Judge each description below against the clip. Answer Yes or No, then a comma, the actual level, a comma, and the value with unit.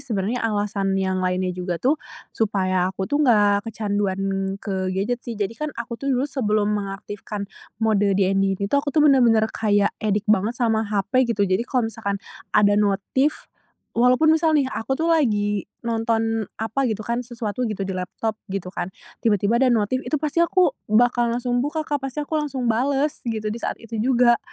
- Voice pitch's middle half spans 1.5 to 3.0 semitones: No, average, 3.8 semitones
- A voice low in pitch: No, high, 220 Hz